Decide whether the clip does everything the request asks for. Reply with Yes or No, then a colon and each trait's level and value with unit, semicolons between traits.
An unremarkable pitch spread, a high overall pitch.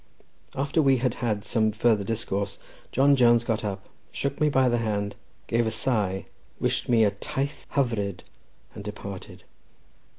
No: average, 3.9 semitones; low, 115 Hz